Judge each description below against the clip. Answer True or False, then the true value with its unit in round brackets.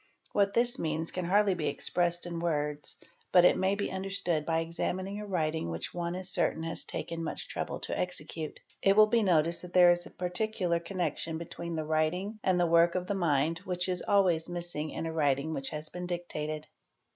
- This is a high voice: False (175 Hz)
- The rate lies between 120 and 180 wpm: False (205 wpm)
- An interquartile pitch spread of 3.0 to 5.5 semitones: False (2.5 semitones)